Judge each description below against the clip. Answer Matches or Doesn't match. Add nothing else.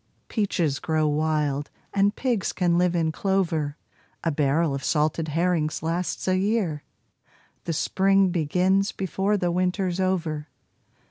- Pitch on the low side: Doesn't match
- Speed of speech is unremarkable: Doesn't match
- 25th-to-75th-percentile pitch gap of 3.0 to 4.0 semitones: Matches